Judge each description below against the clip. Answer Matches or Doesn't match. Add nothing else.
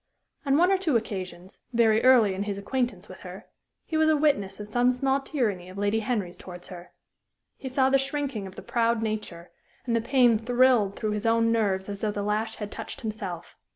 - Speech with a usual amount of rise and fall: Matches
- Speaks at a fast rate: Matches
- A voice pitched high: Matches